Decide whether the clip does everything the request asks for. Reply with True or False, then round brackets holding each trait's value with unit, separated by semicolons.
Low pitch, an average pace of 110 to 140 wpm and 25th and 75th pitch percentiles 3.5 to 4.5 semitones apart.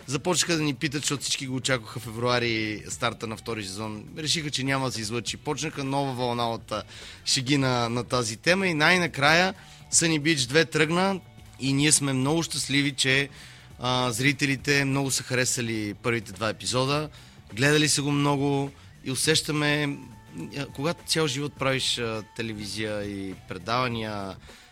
False (130 Hz; 150 wpm; 4.1 semitones)